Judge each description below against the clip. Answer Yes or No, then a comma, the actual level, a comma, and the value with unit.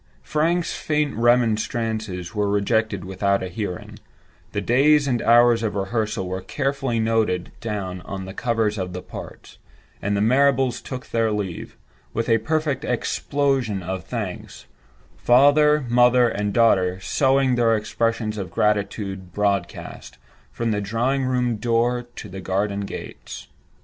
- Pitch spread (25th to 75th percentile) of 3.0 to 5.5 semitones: Yes, average, 3.8 semitones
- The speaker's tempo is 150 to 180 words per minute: No, slow, 135 wpm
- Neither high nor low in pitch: No, low, 115 Hz